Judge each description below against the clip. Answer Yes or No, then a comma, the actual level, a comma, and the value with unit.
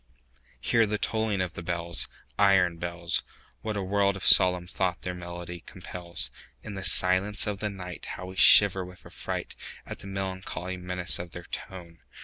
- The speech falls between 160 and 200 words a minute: No, average, 145 wpm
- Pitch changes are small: Yes, narrow, 1.9 semitones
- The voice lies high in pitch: No, very low, 90 Hz